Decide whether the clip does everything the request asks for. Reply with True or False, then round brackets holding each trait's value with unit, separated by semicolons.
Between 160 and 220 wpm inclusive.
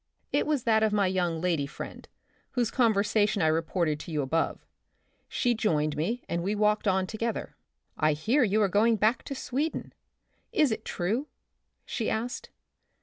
True (170 wpm)